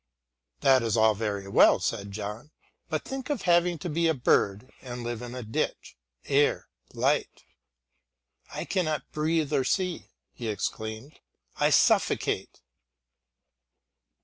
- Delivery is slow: Yes, slow, 130 wpm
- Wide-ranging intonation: Yes, wide, 6.6 semitones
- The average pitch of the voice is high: No, low, 130 Hz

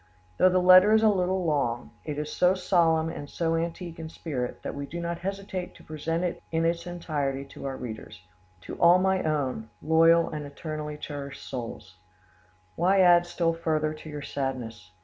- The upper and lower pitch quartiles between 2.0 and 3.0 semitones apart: No, average, 3.6 semitones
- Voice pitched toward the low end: No, medium, 160 Hz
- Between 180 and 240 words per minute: Yes, average, 185 wpm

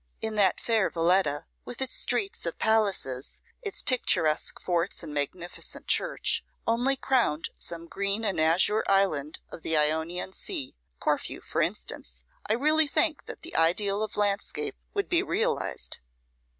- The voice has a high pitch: Yes, high, 195 Hz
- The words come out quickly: No, average, 145 wpm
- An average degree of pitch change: No, wide, 7.0 semitones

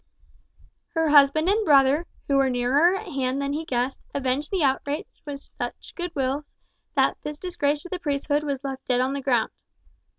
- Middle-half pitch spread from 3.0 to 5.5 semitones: No, narrow, 2.6 semitones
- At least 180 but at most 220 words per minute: Yes, average, 185 wpm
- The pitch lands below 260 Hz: No, very high, 285 Hz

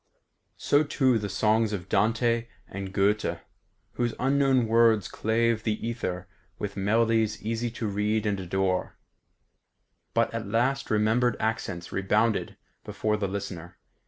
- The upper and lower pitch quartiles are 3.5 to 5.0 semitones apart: No, narrow, 2.6 semitones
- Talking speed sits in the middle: No, slow, 130 wpm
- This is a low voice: Yes, low, 110 Hz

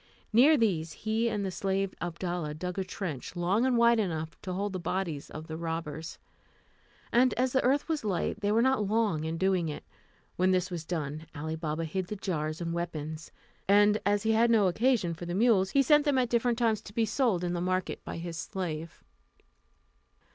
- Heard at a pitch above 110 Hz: Yes, medium, 185 Hz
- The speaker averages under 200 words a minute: No, fast, 205 wpm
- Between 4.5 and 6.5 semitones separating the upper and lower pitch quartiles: Yes, average, 5.1 semitones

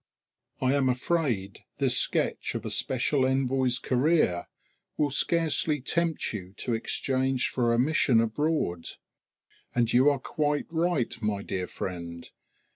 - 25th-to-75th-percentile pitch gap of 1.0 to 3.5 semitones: No, average, 4.6 semitones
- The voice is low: Yes, low, 130 Hz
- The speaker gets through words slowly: Yes, slow, 130 wpm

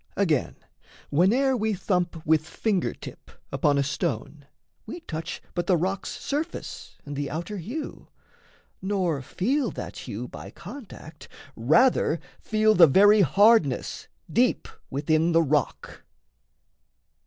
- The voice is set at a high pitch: No, medium, 175 Hz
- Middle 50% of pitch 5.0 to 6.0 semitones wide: Yes, wide, 5.6 semitones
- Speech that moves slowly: Yes, slow, 120 wpm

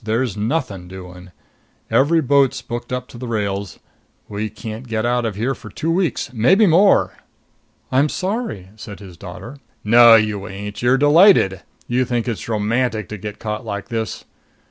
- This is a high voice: No, low, 115 Hz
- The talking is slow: No, average, 165 wpm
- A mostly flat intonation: No, average, 4.0 semitones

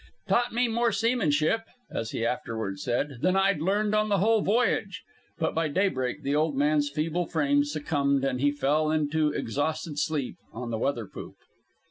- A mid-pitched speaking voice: Yes, medium, 155 Hz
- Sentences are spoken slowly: No, average, 175 wpm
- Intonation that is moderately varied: No, wide, 5.7 semitones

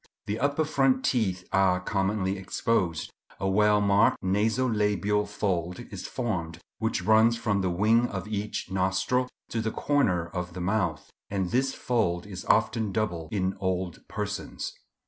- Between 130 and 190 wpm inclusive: Yes, average, 150 wpm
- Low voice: Yes, low, 100 Hz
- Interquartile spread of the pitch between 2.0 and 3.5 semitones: Yes, average, 3.2 semitones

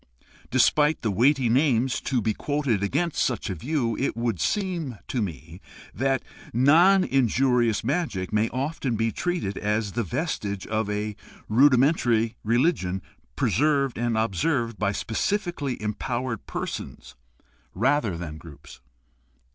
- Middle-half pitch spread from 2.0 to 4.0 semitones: No, average, 5.0 semitones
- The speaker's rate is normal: No, slow, 130 wpm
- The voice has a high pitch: No, low, 120 Hz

